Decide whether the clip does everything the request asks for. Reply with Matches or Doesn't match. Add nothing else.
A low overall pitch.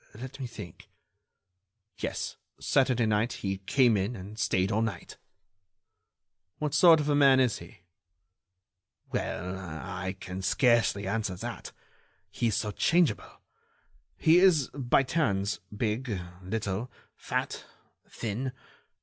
Matches